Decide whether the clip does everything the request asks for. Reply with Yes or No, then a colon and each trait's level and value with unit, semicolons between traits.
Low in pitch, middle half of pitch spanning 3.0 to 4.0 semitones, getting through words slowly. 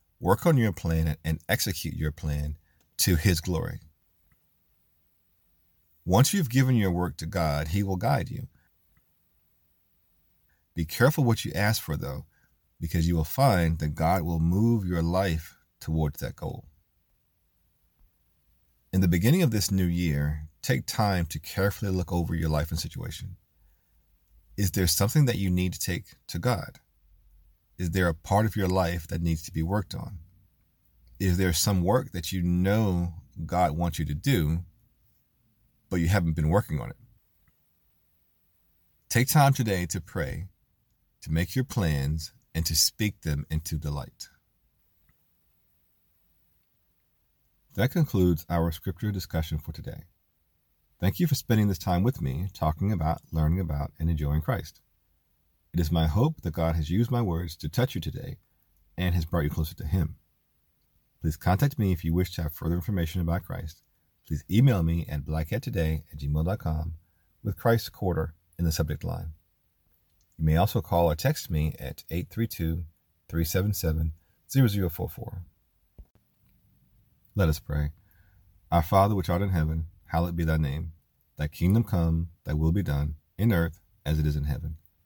No: very low, 85 Hz; average, 3.3 semitones; average, 155 wpm